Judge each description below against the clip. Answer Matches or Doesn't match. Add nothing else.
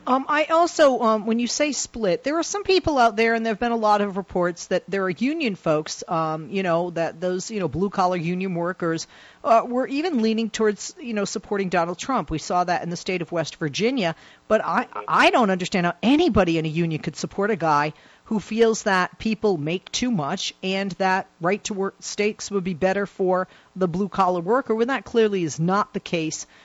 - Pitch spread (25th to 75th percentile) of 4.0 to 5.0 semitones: Matches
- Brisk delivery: Matches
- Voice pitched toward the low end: Doesn't match